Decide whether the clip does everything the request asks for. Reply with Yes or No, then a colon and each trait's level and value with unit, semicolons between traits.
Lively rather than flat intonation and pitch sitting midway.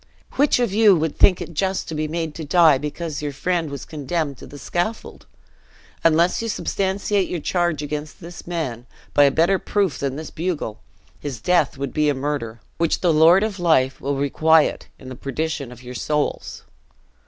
No: average, 3.8 semitones; medium, 155 Hz